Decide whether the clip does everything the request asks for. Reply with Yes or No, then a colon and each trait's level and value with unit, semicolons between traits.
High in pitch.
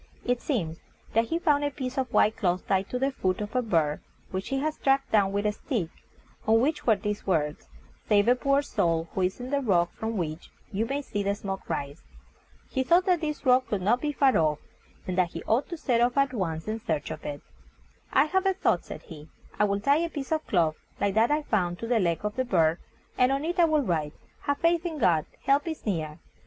Yes: high, 225 Hz